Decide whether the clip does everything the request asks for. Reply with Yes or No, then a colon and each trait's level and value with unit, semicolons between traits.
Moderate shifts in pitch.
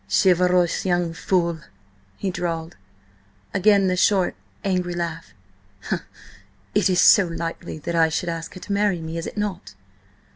No: narrow, 2.2 semitones